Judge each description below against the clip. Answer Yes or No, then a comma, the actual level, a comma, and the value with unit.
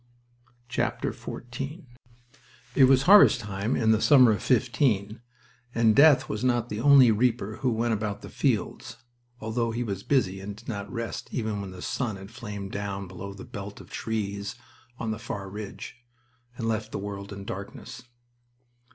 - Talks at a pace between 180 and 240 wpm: No, average, 165 wpm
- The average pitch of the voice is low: Yes, low, 110 Hz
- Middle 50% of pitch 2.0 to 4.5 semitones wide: Yes, average, 3.3 semitones